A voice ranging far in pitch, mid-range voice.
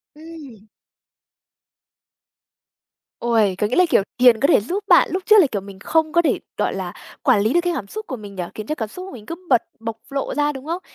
No: wide, 7.4 semitones; very high, 265 Hz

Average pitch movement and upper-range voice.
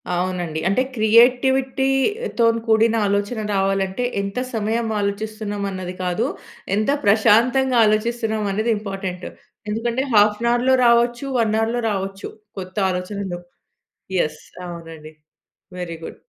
Yes: average, 3.5 semitones; high, 215 Hz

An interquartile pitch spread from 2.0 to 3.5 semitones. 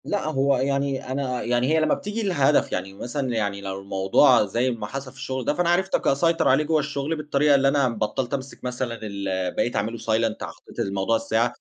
No: average, 4.0 semitones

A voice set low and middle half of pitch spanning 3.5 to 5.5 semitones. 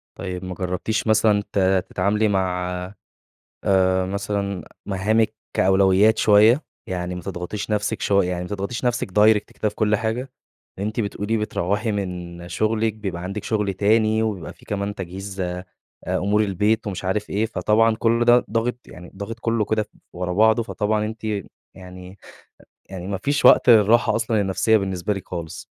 No: low, 105 Hz; average, 2.8 semitones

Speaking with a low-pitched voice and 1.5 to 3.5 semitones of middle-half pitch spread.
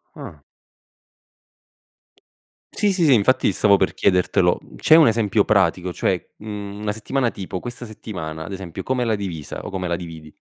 No: low, 100 Hz; average, 4.1 semitones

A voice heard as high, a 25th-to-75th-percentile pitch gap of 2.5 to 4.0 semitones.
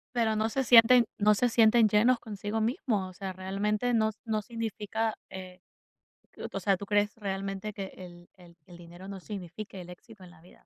Yes: high, 205 Hz; average, 2.9 semitones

